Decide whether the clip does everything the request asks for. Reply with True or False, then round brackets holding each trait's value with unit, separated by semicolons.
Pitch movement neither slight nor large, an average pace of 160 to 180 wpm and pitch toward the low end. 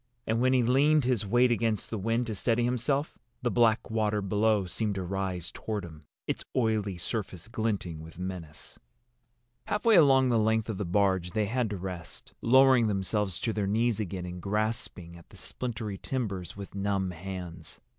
True (3.9 semitones; 175 wpm; 105 Hz)